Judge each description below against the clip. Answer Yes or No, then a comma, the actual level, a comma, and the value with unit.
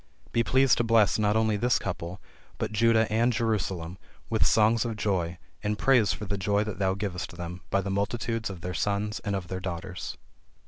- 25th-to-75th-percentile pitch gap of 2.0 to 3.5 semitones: Yes, average, 3.2 semitones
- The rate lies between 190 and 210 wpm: Yes, average, 195 wpm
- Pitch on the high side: No, low, 105 Hz